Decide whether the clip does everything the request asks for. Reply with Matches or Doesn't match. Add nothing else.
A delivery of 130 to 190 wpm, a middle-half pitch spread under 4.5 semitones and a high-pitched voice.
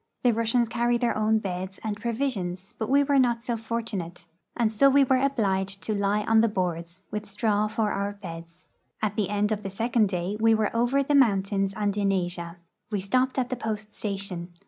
Doesn't match